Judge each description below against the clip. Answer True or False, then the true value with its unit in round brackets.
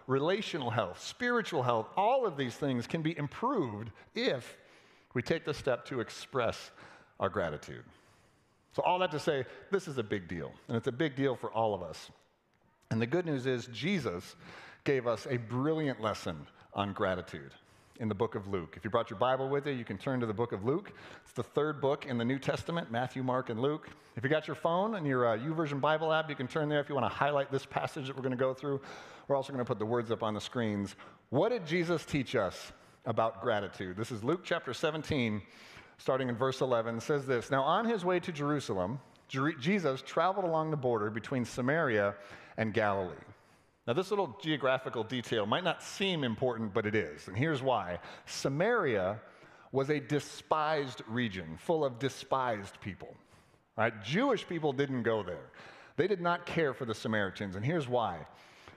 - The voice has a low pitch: True (130 Hz)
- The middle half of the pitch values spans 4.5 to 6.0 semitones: True (4.9 semitones)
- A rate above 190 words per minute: True (200 wpm)